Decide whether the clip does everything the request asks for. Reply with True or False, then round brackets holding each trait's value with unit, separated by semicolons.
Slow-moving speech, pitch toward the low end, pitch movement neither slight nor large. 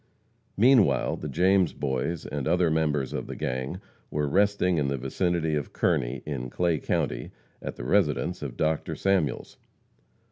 False (150 wpm; 80 Hz; 4.6 semitones)